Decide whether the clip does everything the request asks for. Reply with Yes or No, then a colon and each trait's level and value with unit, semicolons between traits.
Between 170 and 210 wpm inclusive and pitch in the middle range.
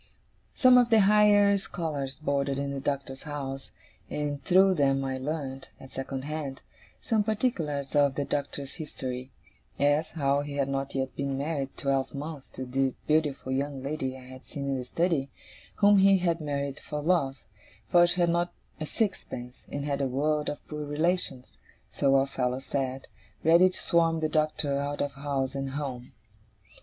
Yes: average, 175 wpm; medium, 145 Hz